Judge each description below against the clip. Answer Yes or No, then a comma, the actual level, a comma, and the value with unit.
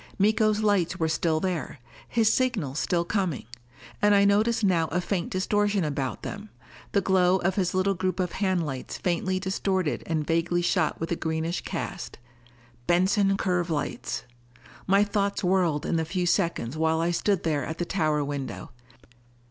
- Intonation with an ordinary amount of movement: Yes, average, 3.5 semitones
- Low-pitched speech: No, medium, 180 Hz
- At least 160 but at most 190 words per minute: Yes, average, 165 wpm